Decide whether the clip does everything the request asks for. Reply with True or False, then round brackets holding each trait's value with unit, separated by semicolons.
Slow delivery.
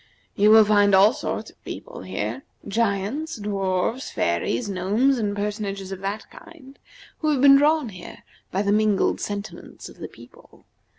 False (160 wpm)